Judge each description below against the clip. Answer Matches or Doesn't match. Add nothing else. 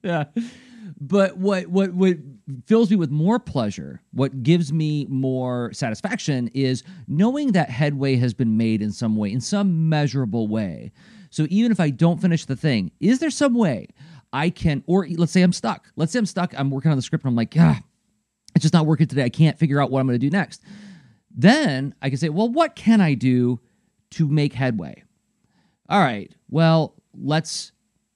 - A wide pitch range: Matches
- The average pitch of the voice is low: Doesn't match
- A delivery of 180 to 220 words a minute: Matches